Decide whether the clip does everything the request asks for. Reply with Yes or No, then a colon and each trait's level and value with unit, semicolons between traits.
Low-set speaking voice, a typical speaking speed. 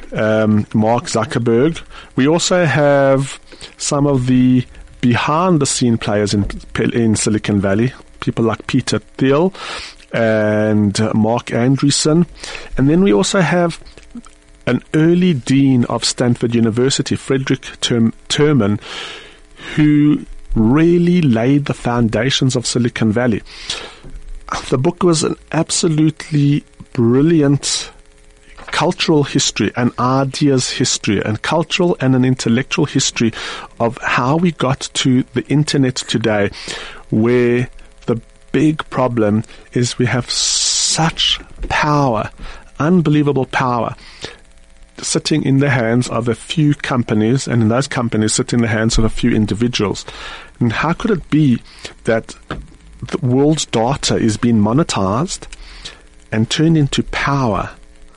No: low, 125 Hz; slow, 120 wpm